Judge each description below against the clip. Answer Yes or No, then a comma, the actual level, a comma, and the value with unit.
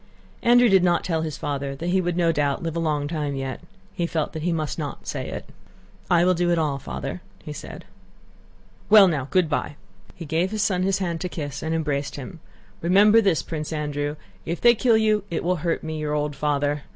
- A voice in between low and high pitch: Yes, medium, 165 Hz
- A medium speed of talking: No, fast, 220 wpm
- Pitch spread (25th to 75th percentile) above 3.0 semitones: Yes, average, 3.5 semitones